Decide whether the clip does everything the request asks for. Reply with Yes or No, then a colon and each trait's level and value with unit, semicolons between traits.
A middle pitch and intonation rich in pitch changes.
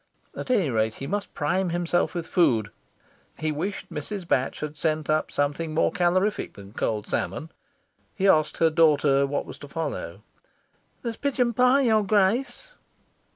Yes: medium, 165 Hz; wide, 5.7 semitones